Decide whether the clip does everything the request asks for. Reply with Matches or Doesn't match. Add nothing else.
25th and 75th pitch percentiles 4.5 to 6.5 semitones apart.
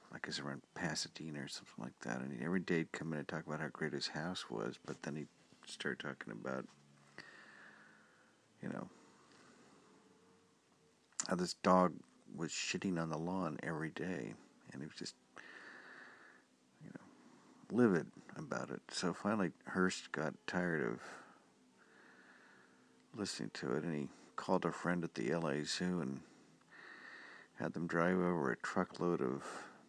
Doesn't match